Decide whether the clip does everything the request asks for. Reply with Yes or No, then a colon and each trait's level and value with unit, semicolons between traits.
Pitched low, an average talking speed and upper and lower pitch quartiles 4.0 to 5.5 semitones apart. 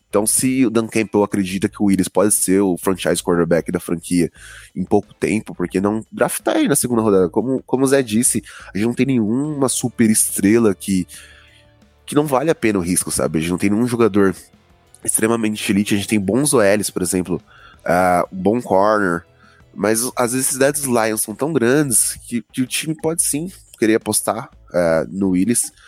Yes: low, 105 Hz; average, 195 wpm; average, 4.6 semitones